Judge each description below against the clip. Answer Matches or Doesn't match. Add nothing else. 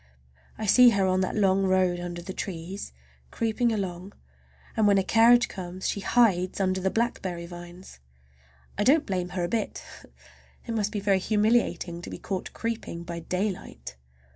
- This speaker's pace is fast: Doesn't match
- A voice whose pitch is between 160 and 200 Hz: Matches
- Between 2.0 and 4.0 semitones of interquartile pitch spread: Matches